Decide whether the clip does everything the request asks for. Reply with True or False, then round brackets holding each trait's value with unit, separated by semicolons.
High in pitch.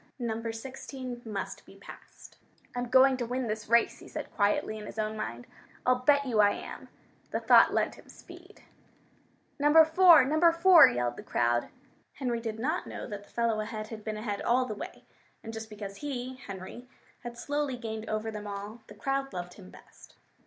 True (230 Hz)